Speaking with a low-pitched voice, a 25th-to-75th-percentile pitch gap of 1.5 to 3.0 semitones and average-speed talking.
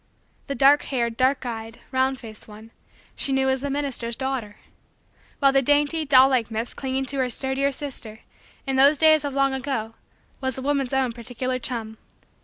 No: very high, 265 Hz; narrow, 2.6 semitones; average, 180 wpm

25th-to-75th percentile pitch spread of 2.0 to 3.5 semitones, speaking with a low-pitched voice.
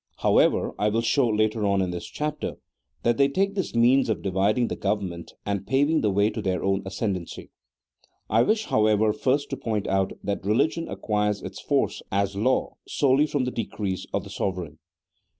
No: average, 4.9 semitones; low, 105 Hz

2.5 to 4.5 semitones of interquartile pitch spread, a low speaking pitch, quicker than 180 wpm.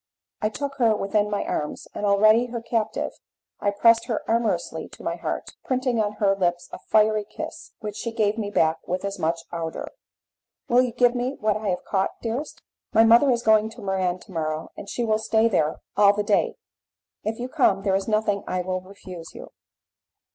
No: average, 3.0 semitones; high, 210 Hz; average, 200 wpm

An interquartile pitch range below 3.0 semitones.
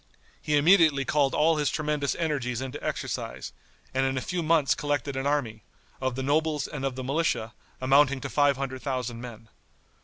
Yes: narrow, 2.5 semitones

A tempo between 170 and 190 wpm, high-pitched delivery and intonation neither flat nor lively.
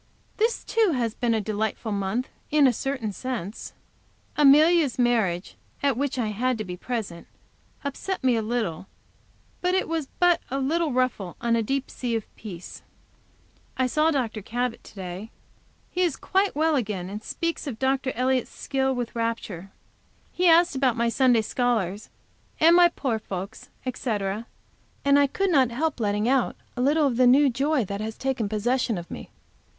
Yes: average, 175 wpm; very high, 250 Hz; average, 4.5 semitones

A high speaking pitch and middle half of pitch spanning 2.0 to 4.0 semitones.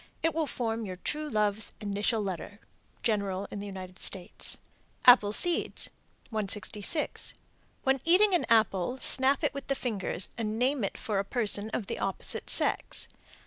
No: high, 215 Hz; average, 4.8 semitones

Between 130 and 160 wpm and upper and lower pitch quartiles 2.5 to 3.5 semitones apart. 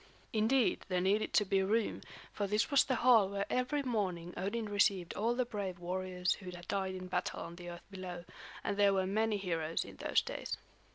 No: fast, 205 wpm; average, 3.1 semitones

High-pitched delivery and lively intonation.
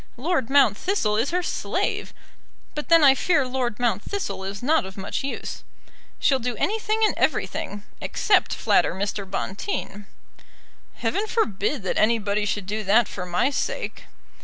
Yes: high, 235 Hz; wide, 6.5 semitones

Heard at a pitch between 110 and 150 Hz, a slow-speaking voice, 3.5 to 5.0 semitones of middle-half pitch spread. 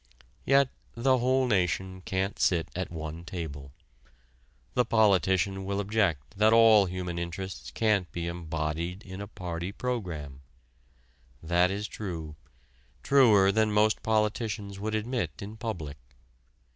No: very low, 95 Hz; slow, 125 wpm; average, 4.1 semitones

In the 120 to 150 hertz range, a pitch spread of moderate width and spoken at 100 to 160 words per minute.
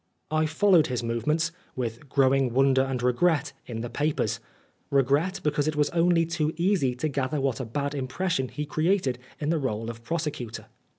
No: medium, 140 Hz; average, 3.7 semitones; average, 175 wpm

